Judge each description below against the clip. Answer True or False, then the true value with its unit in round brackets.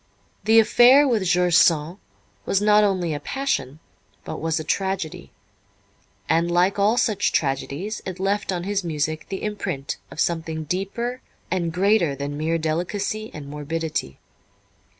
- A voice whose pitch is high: False (175 Hz)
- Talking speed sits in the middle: True (145 wpm)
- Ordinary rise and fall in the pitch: True (4.6 semitones)